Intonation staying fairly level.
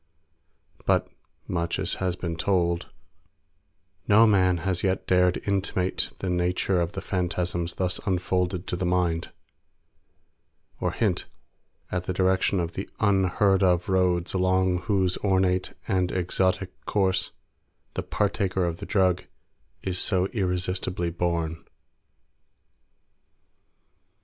Yes: narrow, 1.2 semitones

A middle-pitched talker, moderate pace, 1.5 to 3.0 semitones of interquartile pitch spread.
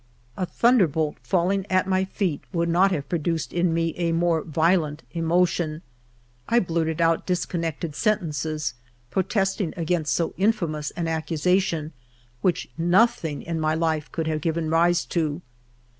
Yes: medium, 170 Hz; average, 145 wpm; narrow, 2.4 semitones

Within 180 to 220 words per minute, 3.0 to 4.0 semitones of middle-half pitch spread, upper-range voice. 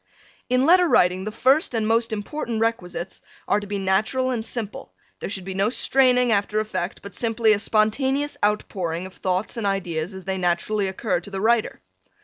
Yes: average, 190 wpm; average, 3.5 semitones; high, 210 Hz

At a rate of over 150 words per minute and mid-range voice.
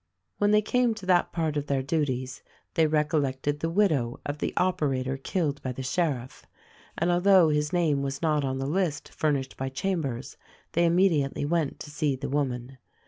Yes: average, 185 wpm; medium, 150 Hz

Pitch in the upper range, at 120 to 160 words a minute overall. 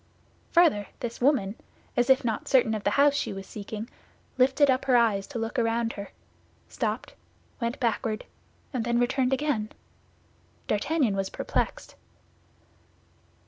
Yes: high, 235 Hz; average, 140 wpm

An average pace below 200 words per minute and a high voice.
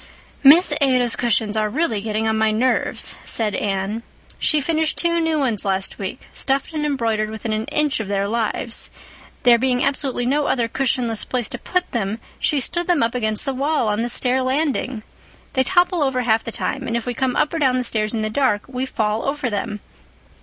No: fast, 205 wpm; high, 245 Hz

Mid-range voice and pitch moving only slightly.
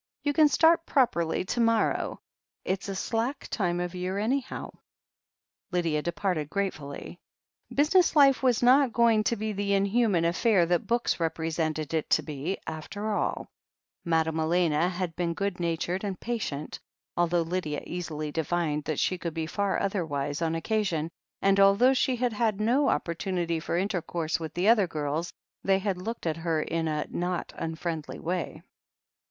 No: medium, 180 Hz; average, 4.7 semitones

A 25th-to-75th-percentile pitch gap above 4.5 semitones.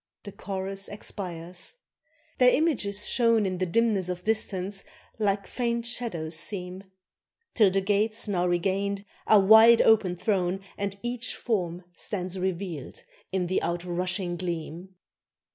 No: average, 3.0 semitones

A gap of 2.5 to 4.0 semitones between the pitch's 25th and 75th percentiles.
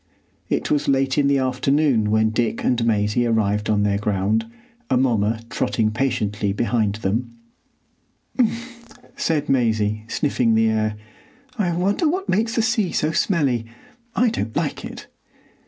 No: wide, 5.5 semitones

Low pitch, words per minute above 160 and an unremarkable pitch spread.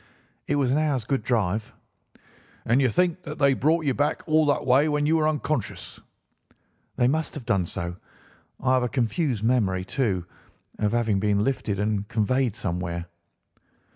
No: low, 125 Hz; average, 170 wpm; wide, 5.9 semitones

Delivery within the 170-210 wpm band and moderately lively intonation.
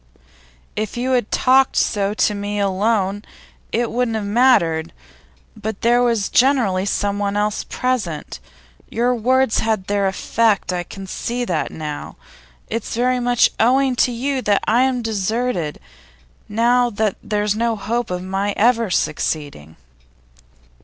No: average, 140 wpm; average, 3.5 semitones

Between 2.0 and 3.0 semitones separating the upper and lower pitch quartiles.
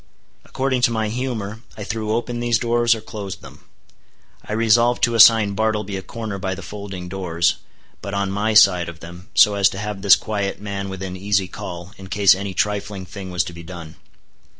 Yes: narrow, 2.6 semitones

